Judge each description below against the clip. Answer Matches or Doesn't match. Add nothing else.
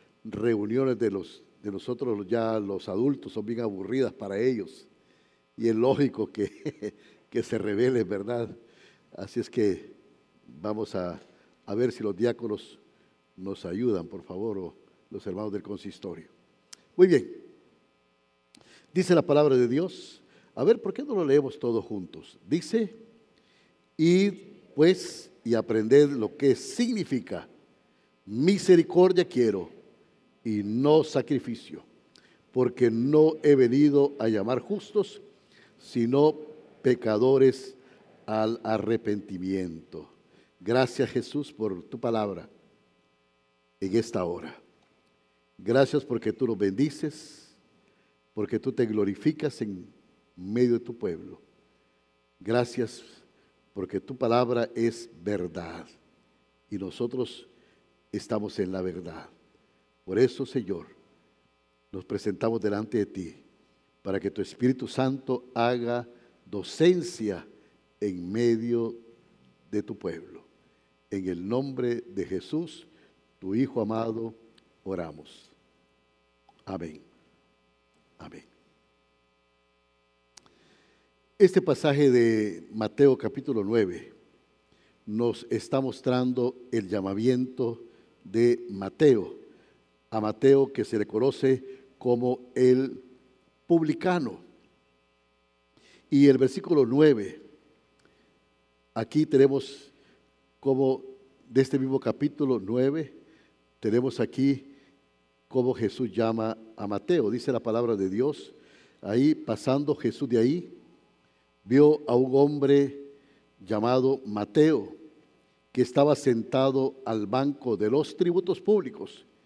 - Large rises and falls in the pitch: Matches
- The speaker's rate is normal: Doesn't match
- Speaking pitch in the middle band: Doesn't match